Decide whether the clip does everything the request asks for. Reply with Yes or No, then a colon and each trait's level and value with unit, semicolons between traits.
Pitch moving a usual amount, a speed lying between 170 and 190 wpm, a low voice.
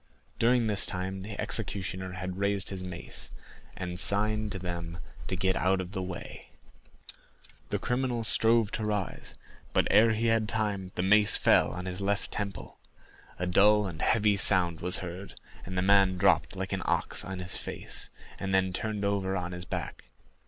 No: narrow, 2.3 semitones; average, 175 wpm; very low, 95 Hz